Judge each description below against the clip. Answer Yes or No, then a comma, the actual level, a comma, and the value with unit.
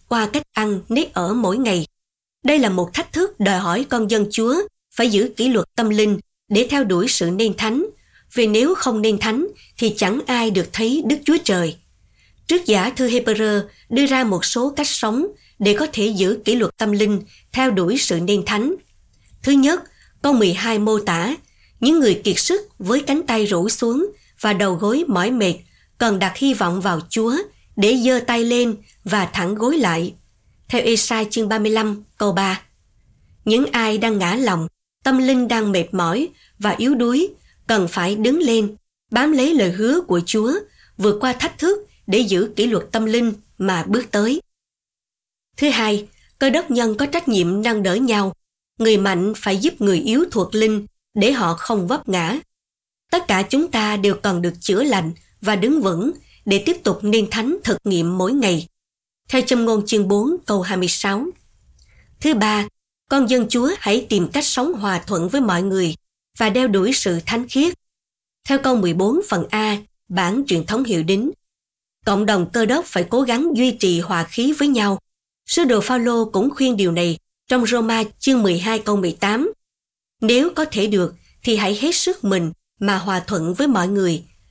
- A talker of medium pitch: No, high, 220 Hz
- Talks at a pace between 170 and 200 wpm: Yes, average, 185 wpm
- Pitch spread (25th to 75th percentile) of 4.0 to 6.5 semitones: Yes, average, 4.7 semitones